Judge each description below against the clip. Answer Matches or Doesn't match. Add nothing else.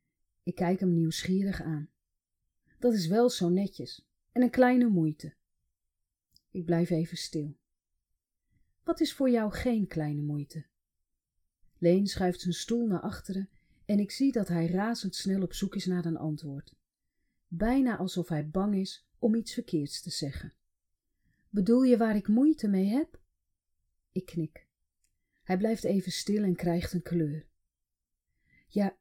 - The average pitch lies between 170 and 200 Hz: Matches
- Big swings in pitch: Doesn't match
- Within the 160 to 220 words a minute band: Doesn't match